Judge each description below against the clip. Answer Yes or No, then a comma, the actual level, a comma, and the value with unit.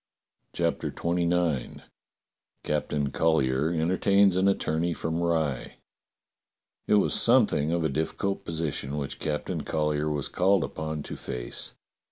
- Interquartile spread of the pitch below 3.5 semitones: Yes, average, 2.9 semitones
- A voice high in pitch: No, very low, 80 Hz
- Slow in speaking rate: Yes, slow, 125 wpm